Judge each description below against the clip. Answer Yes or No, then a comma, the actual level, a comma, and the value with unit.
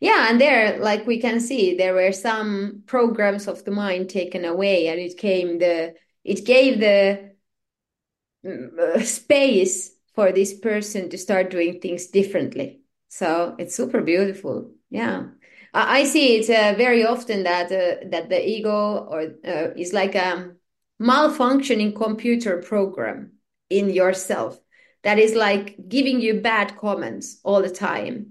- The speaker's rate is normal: Yes, average, 145 wpm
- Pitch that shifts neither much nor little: Yes, average, 3.8 semitones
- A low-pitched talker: No, high, 200 Hz